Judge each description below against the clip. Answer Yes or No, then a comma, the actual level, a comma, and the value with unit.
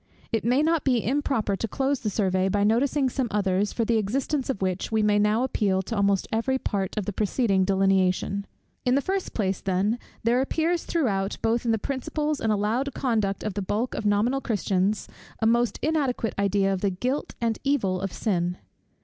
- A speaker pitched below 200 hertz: No, high, 215 Hz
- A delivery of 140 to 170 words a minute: No, average, 195 wpm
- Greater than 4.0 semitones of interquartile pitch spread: Yes, average, 4.7 semitones